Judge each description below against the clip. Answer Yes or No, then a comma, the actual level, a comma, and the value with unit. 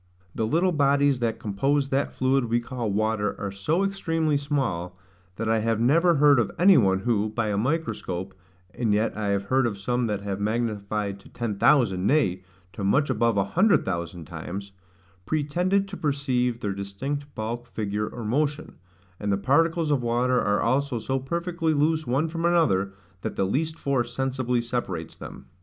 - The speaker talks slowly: No, average, 180 wpm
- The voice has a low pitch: Yes, low, 120 Hz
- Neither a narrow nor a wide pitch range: No, wide, 5.8 semitones